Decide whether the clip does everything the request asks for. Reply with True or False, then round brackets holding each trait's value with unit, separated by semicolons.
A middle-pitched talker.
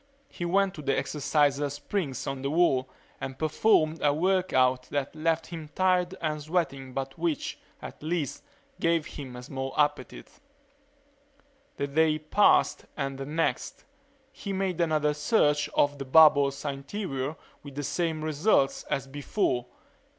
True (150 Hz)